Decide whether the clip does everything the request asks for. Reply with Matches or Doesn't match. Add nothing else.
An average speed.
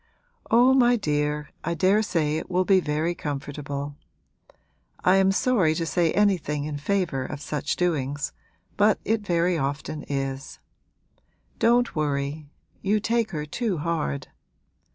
Doesn't match